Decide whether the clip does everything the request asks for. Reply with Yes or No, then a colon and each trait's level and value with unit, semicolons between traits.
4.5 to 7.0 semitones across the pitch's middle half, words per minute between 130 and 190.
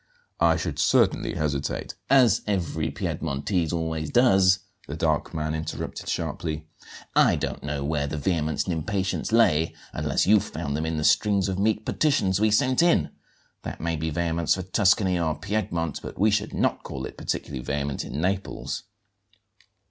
Yes: average, 4.8 semitones; average, 165 wpm